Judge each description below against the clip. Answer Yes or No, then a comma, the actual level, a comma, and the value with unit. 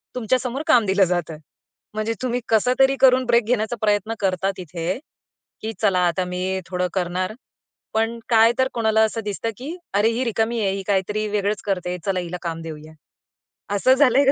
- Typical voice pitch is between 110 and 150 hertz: No, high, 210 Hz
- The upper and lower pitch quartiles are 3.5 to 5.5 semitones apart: Yes, average, 4.2 semitones